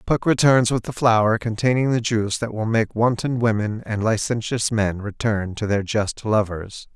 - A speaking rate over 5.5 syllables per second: No, 4.7 syllables/s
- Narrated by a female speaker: No, male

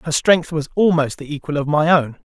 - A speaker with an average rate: No, fast, 235 wpm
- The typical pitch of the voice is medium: Yes, medium, 155 Hz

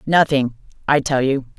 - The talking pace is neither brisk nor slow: Yes, average, 150 wpm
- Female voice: Yes, female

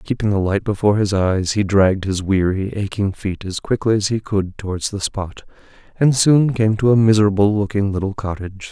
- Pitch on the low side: Yes, low, 100 Hz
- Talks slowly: No, average, 200 wpm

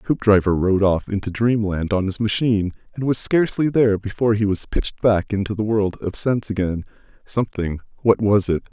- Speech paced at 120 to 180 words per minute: Yes, average, 170 wpm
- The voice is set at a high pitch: No, low, 105 Hz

